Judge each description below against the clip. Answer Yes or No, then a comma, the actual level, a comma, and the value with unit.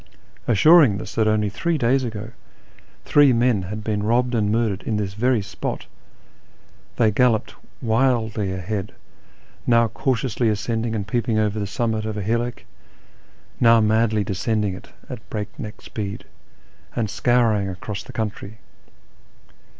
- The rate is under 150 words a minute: Yes, average, 140 wpm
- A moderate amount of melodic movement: No, narrow, 2.2 semitones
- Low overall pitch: Yes, low, 110 Hz